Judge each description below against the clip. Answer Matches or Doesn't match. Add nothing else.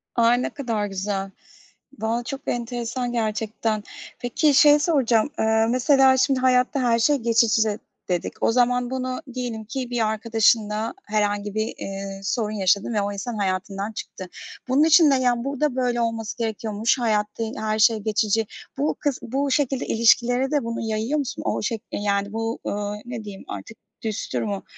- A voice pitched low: Doesn't match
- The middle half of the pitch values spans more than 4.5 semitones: Doesn't match